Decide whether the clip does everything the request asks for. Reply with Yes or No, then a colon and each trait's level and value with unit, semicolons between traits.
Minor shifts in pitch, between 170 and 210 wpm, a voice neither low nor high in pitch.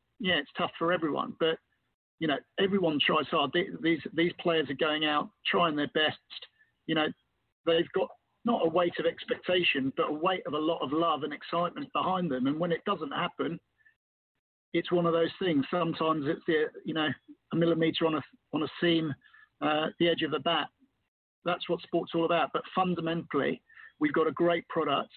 Yes: narrow, 2.3 semitones; average, 195 wpm; medium, 170 Hz